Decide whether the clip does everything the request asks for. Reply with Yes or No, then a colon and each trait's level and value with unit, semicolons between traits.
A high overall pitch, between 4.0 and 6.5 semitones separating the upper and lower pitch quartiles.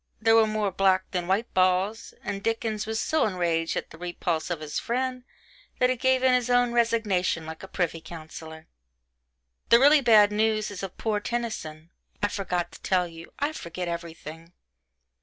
Yes: high, 195 Hz; average, 5.0 semitones